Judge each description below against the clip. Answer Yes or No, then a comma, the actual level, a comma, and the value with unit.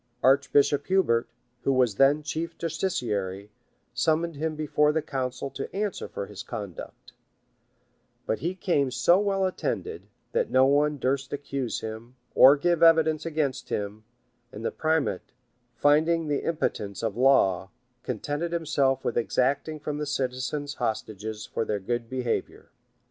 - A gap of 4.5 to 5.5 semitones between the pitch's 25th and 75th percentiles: Yes, average, 5.1 semitones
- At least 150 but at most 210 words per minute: No, average, 140 wpm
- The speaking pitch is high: No, medium, 140 Hz